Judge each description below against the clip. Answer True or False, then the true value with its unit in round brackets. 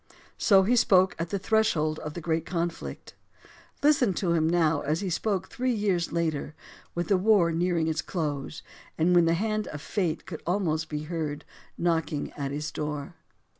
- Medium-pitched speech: True (170 Hz)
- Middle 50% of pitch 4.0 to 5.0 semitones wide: False (3.4 semitones)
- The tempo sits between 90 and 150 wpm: False (175 wpm)